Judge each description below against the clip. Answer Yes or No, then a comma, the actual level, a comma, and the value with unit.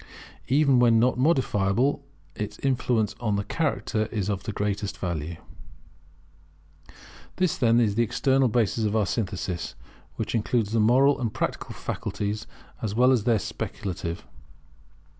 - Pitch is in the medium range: No, low, 110 Hz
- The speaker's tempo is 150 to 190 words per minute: No, average, 140 wpm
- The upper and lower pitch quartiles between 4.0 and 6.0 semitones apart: No, average, 3.6 semitones